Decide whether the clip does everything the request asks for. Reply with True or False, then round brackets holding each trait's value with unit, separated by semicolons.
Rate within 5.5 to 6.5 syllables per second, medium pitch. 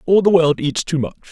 True (5.9 syllables/s; 160 Hz)